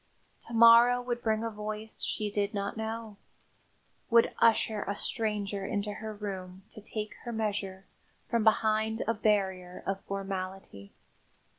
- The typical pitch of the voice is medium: No, high, 210 Hz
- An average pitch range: No, narrow, 2.0 semitones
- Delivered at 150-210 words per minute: No, average, 140 wpm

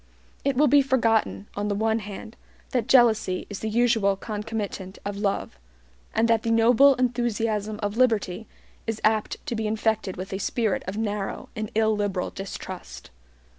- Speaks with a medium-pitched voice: No, high, 220 Hz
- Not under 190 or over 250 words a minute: No, average, 160 wpm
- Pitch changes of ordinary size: No, narrow, 2.2 semitones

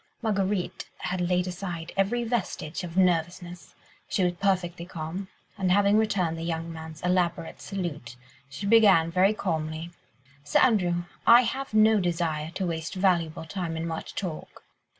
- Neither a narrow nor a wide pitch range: Yes, average, 3.1 semitones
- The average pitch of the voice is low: No, medium, 180 Hz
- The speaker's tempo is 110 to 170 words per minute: Yes, average, 150 wpm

